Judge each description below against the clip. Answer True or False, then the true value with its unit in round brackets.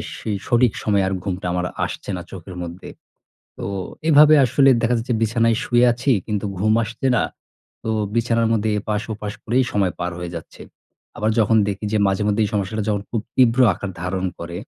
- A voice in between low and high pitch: False (105 Hz)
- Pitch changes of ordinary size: True (3.2 semitones)